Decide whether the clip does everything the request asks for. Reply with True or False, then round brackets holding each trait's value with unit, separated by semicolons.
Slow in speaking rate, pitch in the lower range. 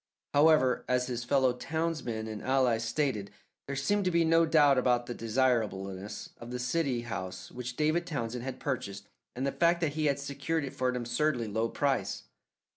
False (185 wpm; 130 Hz)